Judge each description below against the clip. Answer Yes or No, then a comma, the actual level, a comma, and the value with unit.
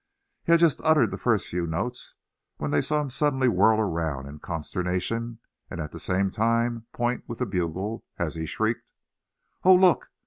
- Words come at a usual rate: Yes, average, 180 wpm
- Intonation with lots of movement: Yes, wide, 6.6 semitones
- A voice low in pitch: Yes, low, 110 Hz